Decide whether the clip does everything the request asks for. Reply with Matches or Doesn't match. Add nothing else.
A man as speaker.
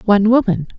Doesn't match